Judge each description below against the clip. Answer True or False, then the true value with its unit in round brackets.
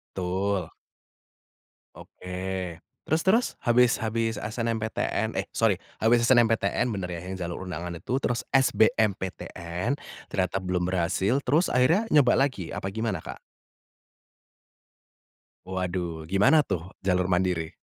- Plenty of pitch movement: False (4.6 semitones)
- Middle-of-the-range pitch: False (95 Hz)